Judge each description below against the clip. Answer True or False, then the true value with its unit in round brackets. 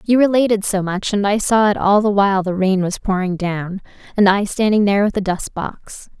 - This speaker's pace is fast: True (230 wpm)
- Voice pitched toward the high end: True (200 Hz)